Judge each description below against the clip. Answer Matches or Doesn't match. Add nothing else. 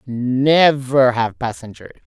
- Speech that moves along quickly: Doesn't match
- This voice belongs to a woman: Matches